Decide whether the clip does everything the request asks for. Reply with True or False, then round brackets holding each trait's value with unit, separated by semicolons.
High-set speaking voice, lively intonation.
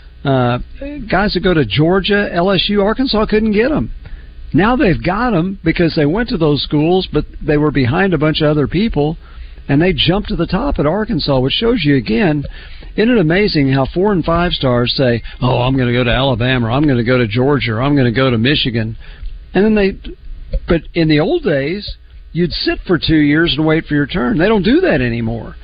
False (150 Hz; 6.3 semitones)